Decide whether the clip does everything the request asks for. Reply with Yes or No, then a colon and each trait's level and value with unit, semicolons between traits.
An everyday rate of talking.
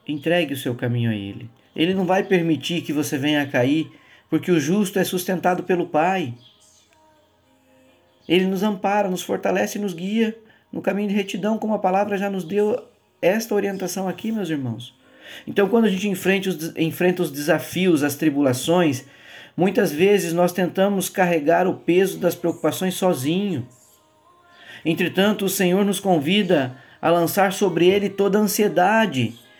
Yes: average, 155 wpm